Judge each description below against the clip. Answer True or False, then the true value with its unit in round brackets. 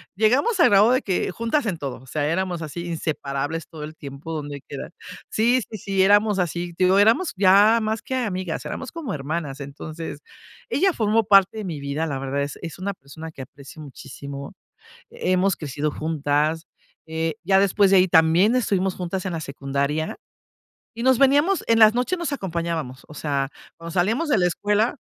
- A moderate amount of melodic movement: False (5.9 semitones)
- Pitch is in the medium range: True (175 Hz)